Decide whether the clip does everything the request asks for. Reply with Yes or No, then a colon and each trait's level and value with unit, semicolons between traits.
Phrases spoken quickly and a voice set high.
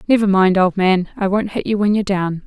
Yes: fast, 270 wpm; high, 195 Hz